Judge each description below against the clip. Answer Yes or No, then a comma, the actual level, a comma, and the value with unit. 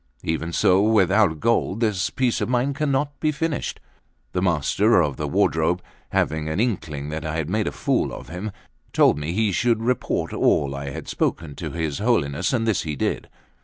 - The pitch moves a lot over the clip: Yes, wide, 6.6 semitones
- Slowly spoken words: No, average, 190 wpm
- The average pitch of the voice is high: No, very low, 95 Hz